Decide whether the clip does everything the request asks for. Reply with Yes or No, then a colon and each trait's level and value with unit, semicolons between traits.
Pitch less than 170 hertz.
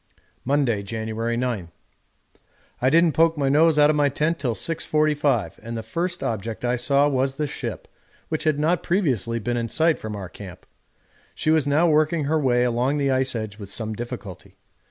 Yes: low, 135 Hz